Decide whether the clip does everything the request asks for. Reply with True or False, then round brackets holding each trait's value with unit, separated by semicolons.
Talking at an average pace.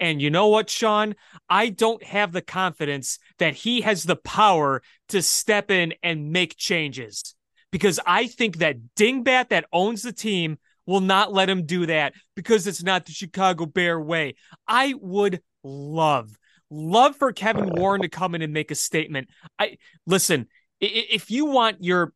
True (170 wpm)